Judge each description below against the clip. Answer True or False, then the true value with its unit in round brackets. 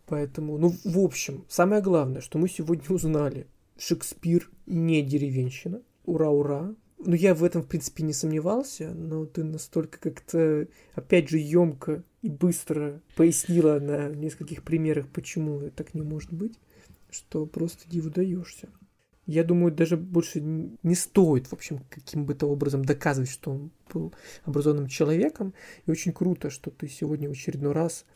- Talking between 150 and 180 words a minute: True (155 wpm)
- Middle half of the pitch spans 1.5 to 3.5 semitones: True (2.7 semitones)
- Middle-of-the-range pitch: True (160 Hz)